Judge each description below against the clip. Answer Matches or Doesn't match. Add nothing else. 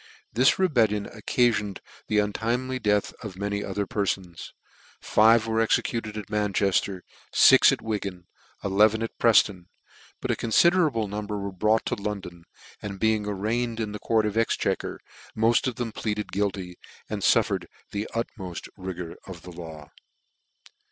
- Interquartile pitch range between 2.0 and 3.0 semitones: Matches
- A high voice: Doesn't match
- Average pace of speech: Matches